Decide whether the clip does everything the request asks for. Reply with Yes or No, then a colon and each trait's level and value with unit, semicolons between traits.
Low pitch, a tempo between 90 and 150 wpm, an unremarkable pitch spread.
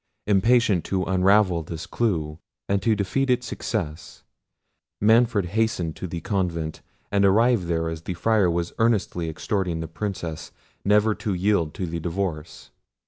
Yes: very low, 95 Hz; average, 145 wpm; average, 4.2 semitones